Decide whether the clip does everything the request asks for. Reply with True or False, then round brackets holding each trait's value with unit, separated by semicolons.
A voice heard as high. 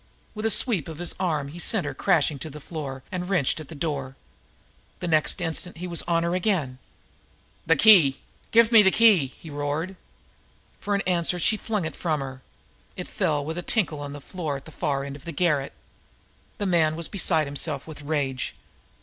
False (160 Hz)